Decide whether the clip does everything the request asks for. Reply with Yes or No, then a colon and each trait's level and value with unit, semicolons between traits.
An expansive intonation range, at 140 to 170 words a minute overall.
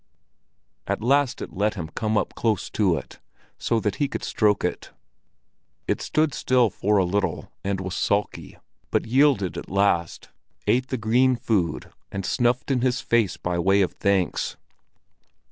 No: average, 4.4 semitones; average, 160 wpm